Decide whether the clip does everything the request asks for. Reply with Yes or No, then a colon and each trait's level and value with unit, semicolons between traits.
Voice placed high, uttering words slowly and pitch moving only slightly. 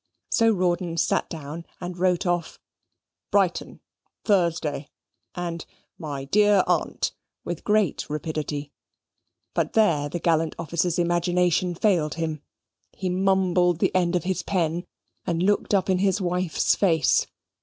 No: medium, 175 Hz; slow, 130 wpm; narrow, 2.3 semitones